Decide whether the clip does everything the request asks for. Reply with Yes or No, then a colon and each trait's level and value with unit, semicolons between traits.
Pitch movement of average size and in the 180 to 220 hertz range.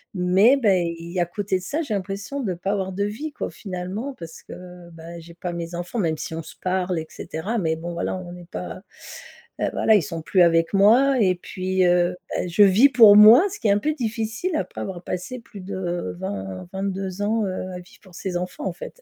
Yes: average, 3.2 semitones; medium, 185 Hz